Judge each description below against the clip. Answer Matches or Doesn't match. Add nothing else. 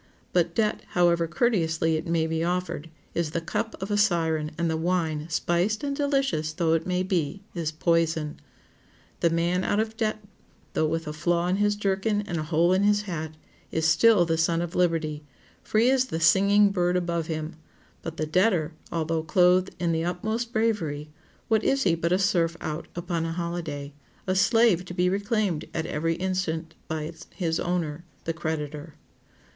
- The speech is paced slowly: Doesn't match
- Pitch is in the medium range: Matches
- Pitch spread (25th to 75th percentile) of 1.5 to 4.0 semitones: Matches